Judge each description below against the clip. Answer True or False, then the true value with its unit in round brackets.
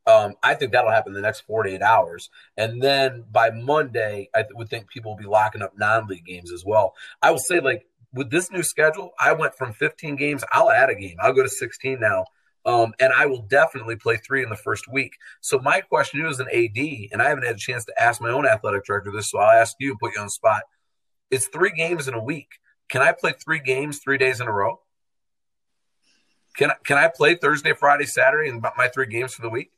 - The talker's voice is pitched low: True (130 Hz)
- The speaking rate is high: True (245 wpm)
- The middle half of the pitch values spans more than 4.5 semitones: True (4.9 semitones)